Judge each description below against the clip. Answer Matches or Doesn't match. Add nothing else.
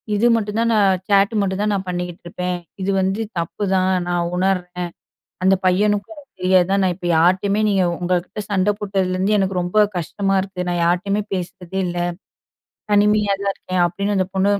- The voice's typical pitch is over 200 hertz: Doesn't match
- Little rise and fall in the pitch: Matches